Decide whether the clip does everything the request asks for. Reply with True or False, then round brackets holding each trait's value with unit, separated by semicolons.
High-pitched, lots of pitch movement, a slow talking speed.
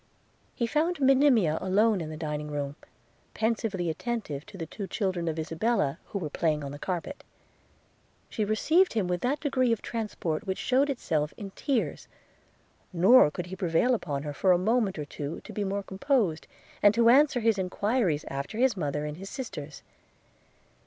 False (195 Hz; 6.8 semitones; 180 wpm)